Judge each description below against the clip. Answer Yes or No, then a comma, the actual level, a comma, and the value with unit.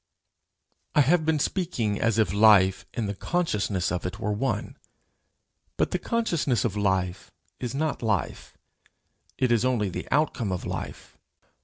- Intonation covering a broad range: Yes, wide, 6.0 semitones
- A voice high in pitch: No, low, 110 Hz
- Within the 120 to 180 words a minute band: Yes, average, 150 wpm